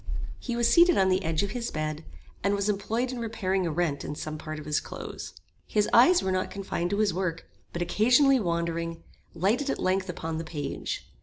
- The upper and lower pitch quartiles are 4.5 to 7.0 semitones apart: Yes, average, 5.1 semitones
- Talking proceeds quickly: Yes, fast, 210 wpm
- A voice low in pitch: No, high, 190 Hz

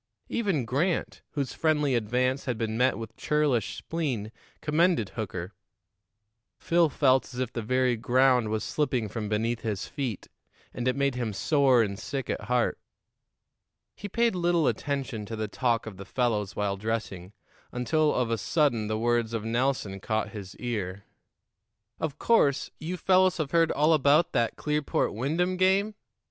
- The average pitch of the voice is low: Yes, low, 125 Hz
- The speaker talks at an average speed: Yes, average, 160 wpm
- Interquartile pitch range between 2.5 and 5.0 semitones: No, wide, 5.4 semitones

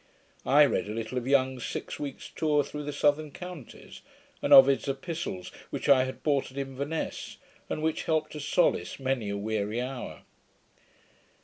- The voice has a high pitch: No, low, 135 Hz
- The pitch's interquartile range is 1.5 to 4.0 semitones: Yes, average, 2.8 semitones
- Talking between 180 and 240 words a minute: No, average, 165 wpm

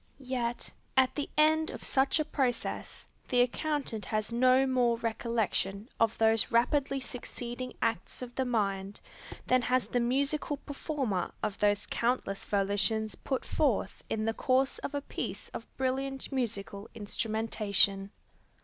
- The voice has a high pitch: Yes, high, 240 Hz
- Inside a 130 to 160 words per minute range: Yes, average, 140 wpm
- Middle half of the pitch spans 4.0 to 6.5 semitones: No, average, 3.5 semitones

